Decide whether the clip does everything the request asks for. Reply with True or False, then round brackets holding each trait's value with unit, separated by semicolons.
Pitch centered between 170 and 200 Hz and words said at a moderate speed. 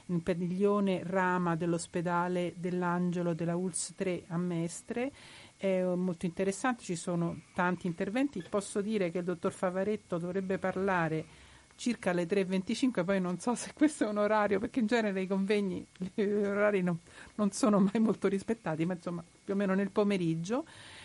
True (190 Hz; 160 wpm)